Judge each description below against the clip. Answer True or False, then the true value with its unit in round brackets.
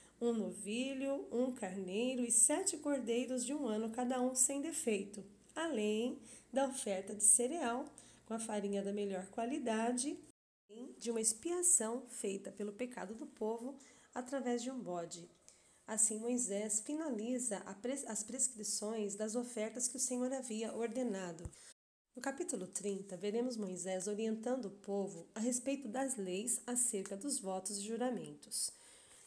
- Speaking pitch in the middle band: False (235 Hz)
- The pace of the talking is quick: False (135 wpm)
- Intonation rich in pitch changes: False (3.7 semitones)